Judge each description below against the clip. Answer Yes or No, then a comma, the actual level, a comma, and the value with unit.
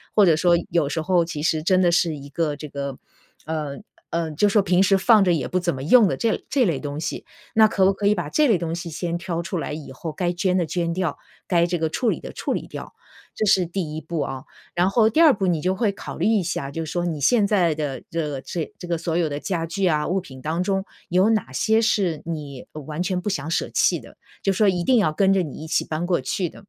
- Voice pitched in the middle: Yes, medium, 175 Hz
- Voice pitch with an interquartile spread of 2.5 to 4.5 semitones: Yes, average, 3.5 semitones